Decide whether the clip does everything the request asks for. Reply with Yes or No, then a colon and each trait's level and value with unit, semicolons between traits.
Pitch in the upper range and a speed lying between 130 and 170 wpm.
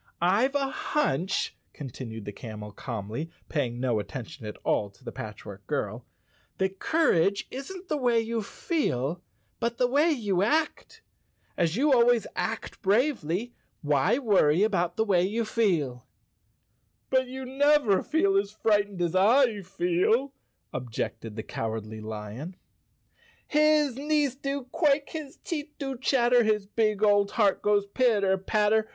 Yes: high, 205 Hz; average, 145 wpm